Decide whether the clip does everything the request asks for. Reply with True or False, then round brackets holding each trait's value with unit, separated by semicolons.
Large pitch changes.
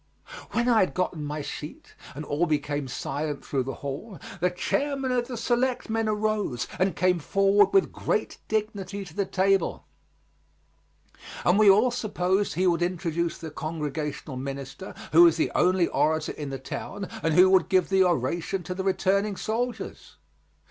False (4.9 semitones)